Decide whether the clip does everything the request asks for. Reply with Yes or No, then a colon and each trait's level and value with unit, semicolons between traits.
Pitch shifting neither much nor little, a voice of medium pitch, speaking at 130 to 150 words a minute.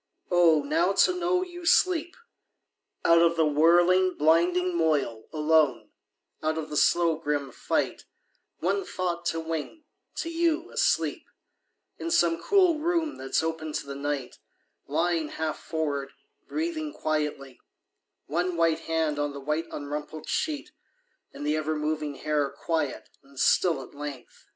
Yes: average, 3.6 semitones; medium, 160 Hz; average, 140 wpm